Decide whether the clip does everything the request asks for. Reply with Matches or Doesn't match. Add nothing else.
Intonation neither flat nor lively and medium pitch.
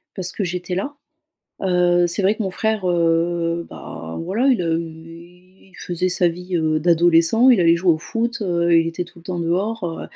Doesn't match